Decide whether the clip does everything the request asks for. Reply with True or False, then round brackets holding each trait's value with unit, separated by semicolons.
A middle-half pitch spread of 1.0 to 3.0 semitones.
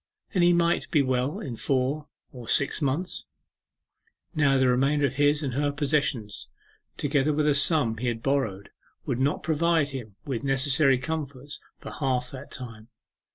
True (2.7 semitones)